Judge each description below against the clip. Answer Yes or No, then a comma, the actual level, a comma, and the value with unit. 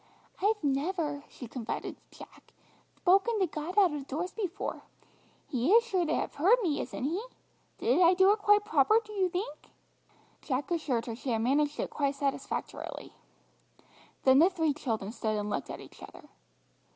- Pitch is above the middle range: Yes, very high, 310 Hz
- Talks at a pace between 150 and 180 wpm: Yes, average, 175 wpm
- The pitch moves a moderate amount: No, wide, 6.0 semitones